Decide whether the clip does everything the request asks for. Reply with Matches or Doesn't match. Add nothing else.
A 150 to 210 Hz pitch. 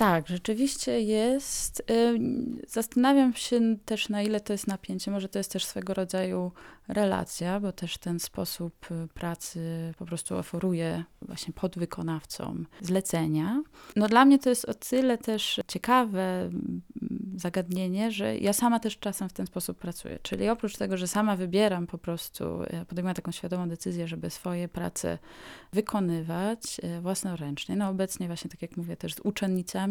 Matches